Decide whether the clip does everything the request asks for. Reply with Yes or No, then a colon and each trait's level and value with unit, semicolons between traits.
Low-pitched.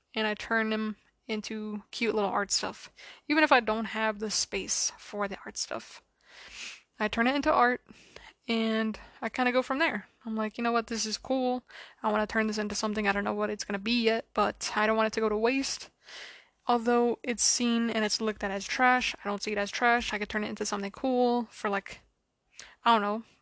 No: high, 220 Hz